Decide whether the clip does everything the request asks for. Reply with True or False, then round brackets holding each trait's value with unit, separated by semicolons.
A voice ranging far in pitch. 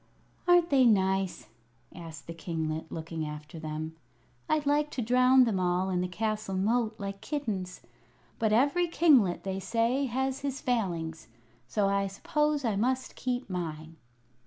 True (6.5 semitones)